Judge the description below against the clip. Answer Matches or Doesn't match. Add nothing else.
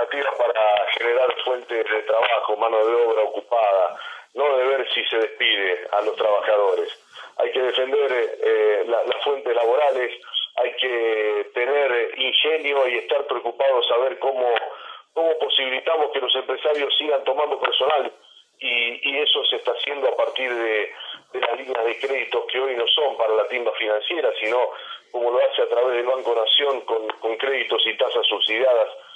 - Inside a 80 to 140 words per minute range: Doesn't match